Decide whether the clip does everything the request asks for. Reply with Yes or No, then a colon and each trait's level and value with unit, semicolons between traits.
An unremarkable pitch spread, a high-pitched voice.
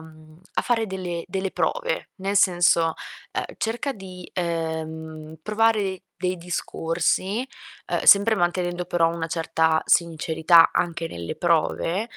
No: average, 3.0 semitones; medium, 175 Hz